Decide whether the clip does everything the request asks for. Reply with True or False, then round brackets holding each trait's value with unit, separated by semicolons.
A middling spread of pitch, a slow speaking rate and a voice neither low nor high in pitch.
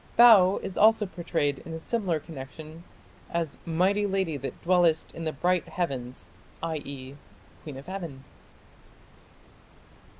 True (4.4 semitones; 125 wpm; 165 Hz)